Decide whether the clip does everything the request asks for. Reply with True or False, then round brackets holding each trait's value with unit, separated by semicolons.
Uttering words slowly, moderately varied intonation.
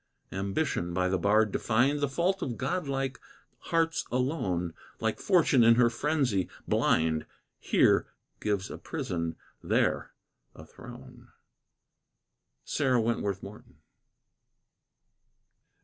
False (100 wpm; 6.3 semitones)